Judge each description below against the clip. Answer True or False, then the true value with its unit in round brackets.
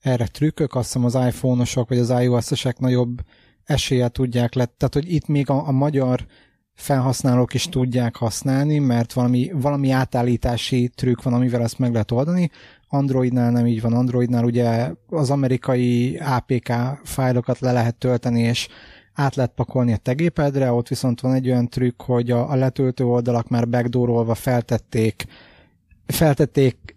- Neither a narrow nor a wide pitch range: False (1.7 semitones)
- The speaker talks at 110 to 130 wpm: False (150 wpm)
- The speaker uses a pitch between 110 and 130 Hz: True (125 Hz)